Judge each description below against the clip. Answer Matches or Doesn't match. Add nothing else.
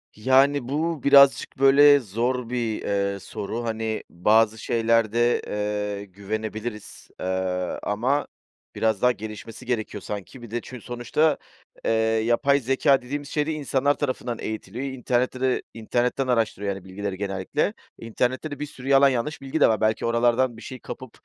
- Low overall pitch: Matches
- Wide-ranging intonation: Doesn't match